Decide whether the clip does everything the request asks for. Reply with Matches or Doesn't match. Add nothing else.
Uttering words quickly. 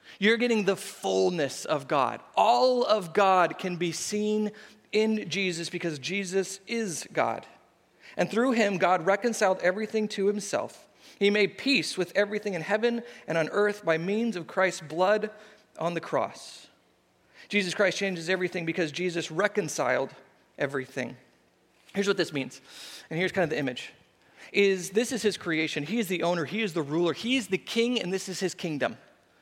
Doesn't match